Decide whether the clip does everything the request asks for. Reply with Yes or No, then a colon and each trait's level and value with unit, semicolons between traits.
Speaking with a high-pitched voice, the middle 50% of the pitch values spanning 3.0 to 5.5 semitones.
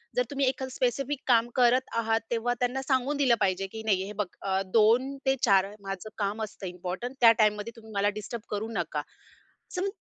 Yes: high, 230 Hz; average, 4.2 semitones